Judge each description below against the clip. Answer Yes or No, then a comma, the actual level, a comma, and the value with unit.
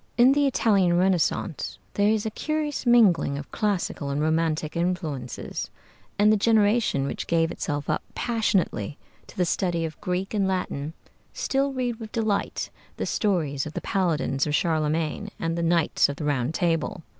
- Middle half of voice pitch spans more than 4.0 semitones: Yes, wide, 5.5 semitones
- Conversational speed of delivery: Yes, average, 165 wpm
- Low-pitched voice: No, medium, 175 Hz